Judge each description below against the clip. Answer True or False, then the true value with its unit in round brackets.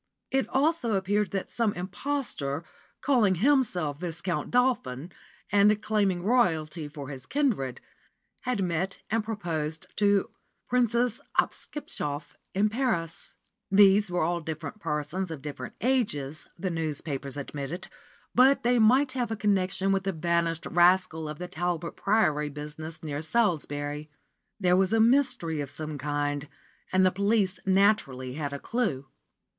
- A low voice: False (180 Hz)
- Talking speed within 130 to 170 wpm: True (135 wpm)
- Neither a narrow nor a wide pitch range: False (6.0 semitones)